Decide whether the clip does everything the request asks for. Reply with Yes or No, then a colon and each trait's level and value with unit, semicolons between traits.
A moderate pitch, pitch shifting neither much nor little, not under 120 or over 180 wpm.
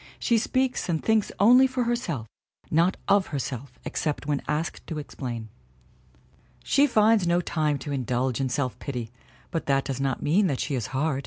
No: medium, 150 Hz; wide, 7.3 semitones; average, 175 wpm